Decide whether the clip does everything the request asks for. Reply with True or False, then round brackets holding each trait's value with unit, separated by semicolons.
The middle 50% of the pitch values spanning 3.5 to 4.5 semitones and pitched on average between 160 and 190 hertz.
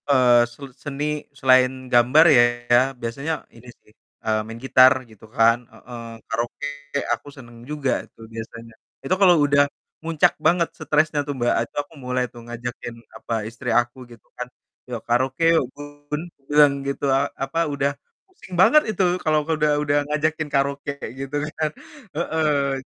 False (3.8 semitones; 140 Hz)